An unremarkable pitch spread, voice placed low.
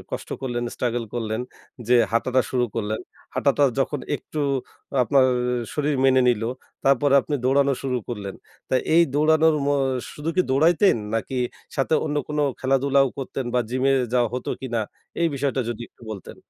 Yes: average, 3.0 semitones; low, 130 Hz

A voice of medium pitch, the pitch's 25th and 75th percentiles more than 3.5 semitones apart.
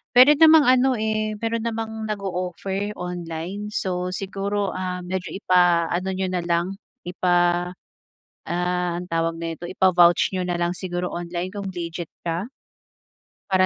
No: medium, 180 Hz; narrow, 2.5 semitones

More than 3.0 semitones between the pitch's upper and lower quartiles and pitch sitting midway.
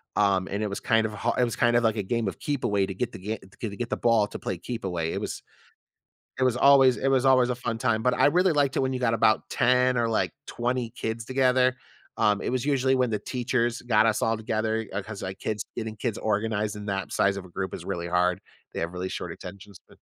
No: average, 3.6 semitones; low, 115 Hz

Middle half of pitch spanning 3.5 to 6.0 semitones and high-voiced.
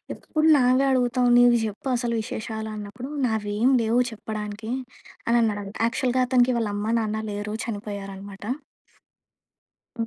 No: average, 2.9 semitones; high, 220 Hz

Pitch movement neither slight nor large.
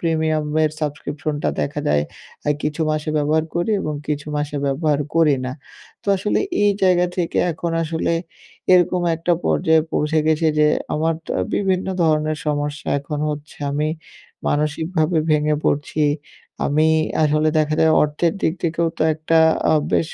No: narrow, 1.5 semitones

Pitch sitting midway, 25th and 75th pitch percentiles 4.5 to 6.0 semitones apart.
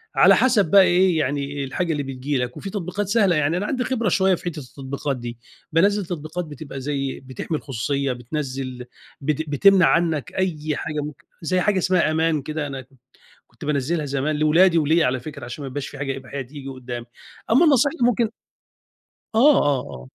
Yes: medium, 150 Hz; average, 5.0 semitones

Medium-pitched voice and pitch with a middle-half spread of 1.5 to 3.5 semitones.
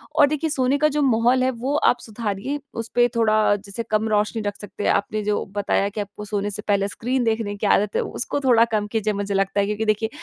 No: high, 215 Hz; average, 2.9 semitones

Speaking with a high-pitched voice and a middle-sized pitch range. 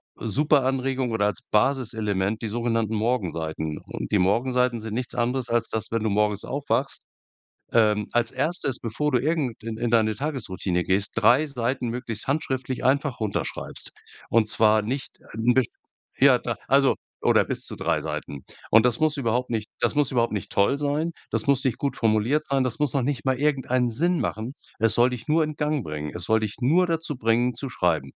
No: low, 120 Hz; average, 3.9 semitones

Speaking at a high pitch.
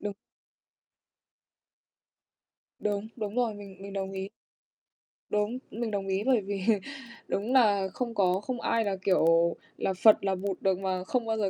Yes: high, 200 Hz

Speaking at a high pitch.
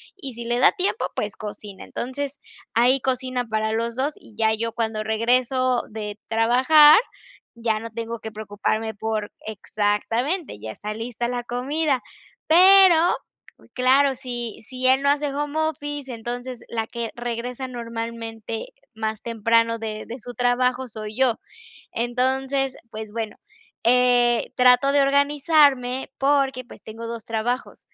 Yes: high, 245 Hz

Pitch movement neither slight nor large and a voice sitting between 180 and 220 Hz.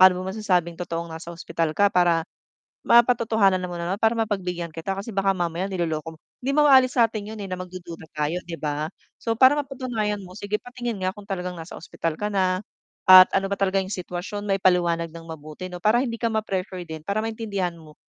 Yes: average, 3.7 semitones; medium, 185 Hz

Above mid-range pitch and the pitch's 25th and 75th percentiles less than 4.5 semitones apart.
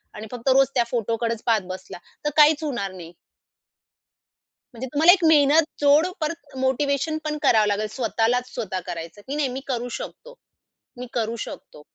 No: very high, 250 Hz; average, 5.0 semitones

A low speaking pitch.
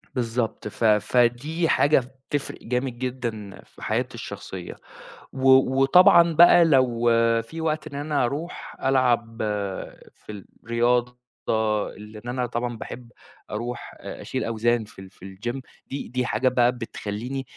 Yes: low, 125 Hz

